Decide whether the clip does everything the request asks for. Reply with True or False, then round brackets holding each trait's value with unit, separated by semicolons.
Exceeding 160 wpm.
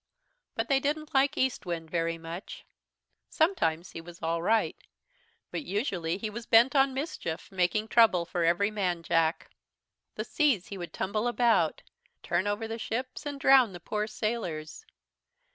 False (155 wpm)